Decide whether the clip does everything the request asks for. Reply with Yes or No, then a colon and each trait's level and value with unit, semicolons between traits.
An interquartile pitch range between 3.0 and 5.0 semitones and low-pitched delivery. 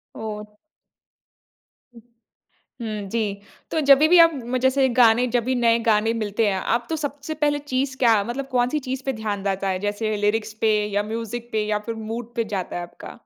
No: average, 3.7 semitones; high, 230 Hz